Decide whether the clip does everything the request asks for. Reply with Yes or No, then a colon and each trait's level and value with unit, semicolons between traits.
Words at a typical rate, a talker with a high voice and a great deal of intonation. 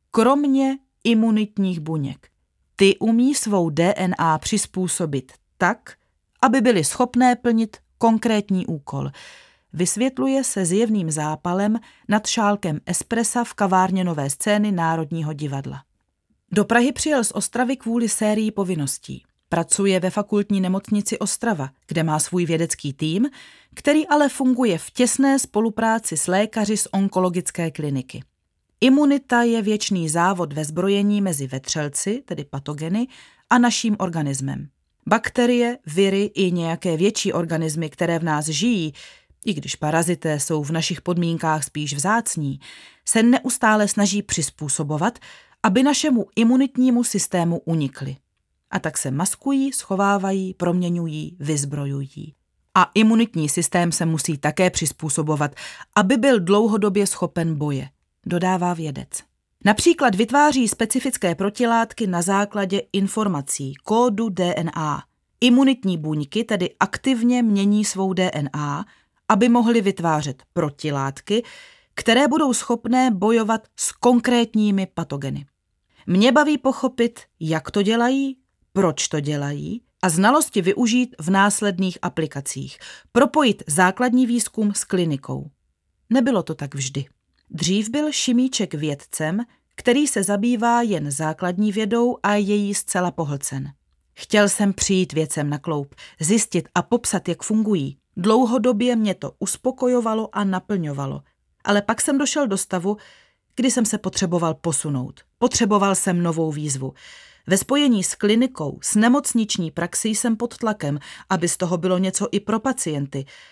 Yes: average, 125 wpm; high, 195 Hz; wide, 6.3 semitones